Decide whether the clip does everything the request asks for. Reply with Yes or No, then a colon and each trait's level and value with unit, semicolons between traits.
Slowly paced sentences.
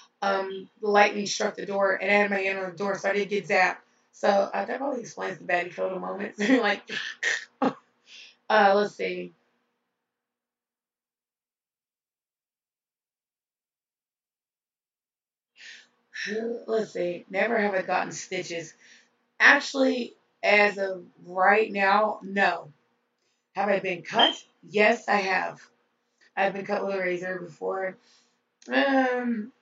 Yes: slow, 120 wpm